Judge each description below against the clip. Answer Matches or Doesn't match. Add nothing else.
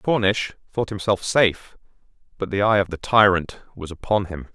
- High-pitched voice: Doesn't match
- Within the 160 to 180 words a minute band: Matches